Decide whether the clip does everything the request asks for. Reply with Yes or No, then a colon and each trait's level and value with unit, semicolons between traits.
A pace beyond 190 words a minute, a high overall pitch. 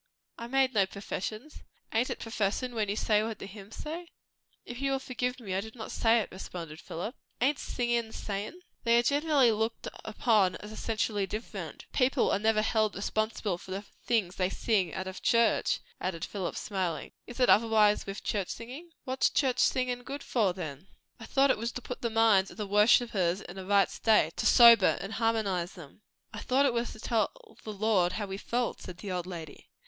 Yes: average, 200 wpm; high, 220 Hz